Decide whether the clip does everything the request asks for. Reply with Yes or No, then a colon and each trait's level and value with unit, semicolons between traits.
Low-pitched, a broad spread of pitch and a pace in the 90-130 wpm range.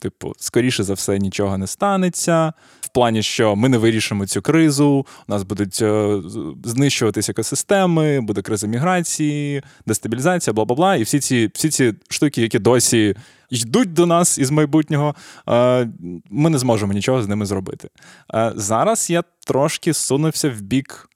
No: low, 125 Hz; wide, 6.2 semitones; fast, 155 wpm